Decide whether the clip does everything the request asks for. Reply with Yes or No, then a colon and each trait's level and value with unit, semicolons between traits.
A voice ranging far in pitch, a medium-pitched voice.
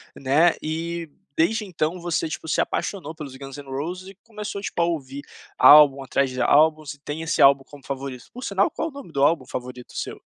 No: average, 3.8 semitones; medium, 155 Hz